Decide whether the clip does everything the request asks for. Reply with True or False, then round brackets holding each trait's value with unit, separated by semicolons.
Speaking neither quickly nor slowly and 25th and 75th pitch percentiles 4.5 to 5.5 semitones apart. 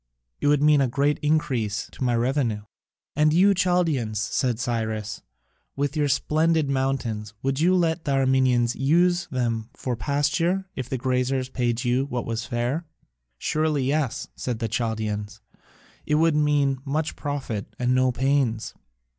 False (150 wpm; 3.9 semitones)